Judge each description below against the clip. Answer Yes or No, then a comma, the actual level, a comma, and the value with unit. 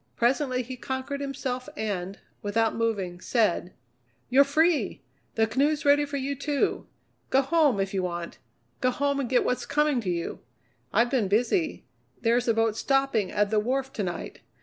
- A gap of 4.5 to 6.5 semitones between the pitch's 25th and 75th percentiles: Yes, average, 4.8 semitones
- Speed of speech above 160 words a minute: Yes, average, 170 wpm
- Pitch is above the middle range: Yes, very high, 250 Hz